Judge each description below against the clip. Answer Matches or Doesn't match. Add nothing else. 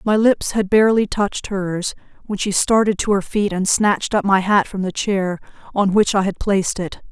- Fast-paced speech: Matches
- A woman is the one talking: Matches